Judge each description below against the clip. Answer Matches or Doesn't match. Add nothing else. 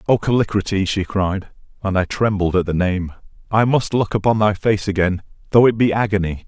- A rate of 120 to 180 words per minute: Doesn't match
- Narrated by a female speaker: Doesn't match